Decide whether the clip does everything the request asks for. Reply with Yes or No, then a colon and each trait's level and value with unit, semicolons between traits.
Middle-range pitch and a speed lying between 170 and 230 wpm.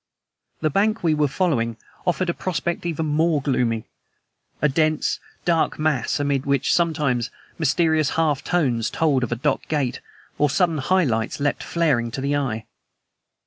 No: medium, 150 Hz; average, 155 wpm